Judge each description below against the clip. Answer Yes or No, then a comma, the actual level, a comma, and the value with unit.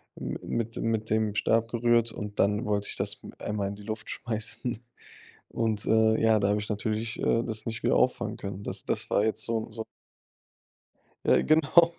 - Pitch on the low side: Yes, low, 110 Hz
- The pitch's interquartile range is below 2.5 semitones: Yes, narrow, 1.6 semitones